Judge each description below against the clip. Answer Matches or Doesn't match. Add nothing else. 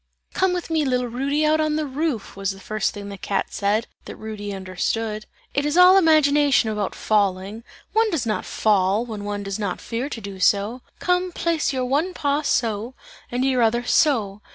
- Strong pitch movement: Matches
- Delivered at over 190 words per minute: Matches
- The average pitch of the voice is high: Matches